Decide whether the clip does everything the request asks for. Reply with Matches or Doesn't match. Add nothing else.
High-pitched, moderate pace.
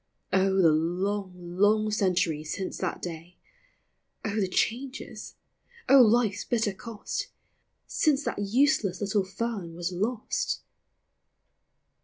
Doesn't match